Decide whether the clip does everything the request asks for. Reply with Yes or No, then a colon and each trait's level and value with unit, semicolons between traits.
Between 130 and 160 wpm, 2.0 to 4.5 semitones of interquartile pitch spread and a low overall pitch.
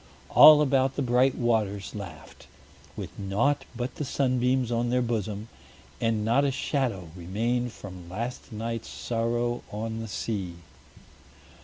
Yes: slow, 135 wpm; average, 3.2 semitones; low, 115 Hz